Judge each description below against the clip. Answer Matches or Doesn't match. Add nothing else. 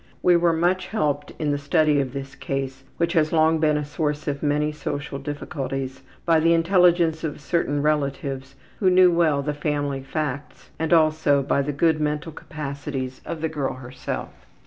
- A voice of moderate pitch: Matches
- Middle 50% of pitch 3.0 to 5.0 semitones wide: Doesn't match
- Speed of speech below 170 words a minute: Doesn't match